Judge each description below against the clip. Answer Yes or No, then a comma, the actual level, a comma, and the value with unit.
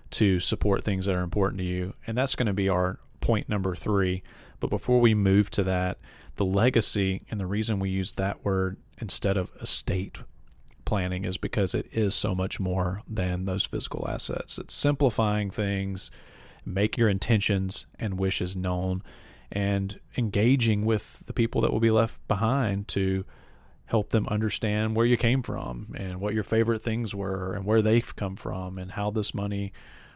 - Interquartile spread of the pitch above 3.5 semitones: No, average, 2.8 semitones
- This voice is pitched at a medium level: No, low, 100 Hz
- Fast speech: No, average, 175 wpm